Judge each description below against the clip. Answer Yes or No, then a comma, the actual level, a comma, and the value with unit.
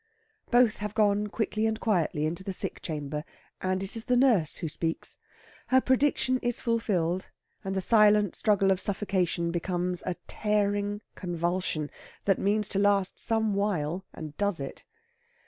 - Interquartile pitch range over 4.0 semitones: No, average, 3.3 semitones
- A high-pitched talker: Yes, high, 200 Hz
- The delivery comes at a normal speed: Yes, average, 155 wpm